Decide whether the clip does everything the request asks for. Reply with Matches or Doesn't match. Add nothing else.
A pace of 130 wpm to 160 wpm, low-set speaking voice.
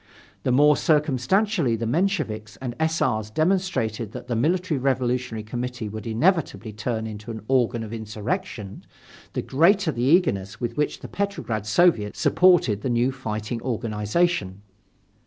Matches